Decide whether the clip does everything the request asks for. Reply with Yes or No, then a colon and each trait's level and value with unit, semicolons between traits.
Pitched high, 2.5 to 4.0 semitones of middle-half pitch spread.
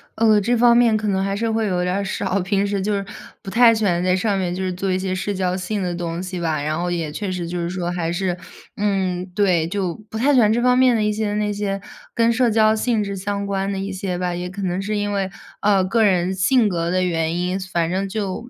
Yes: high, 195 Hz; average, 2.8 semitones